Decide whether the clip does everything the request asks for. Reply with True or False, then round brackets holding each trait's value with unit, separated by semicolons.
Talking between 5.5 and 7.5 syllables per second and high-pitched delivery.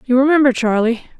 True (6.3 syllables/s; 250 Hz)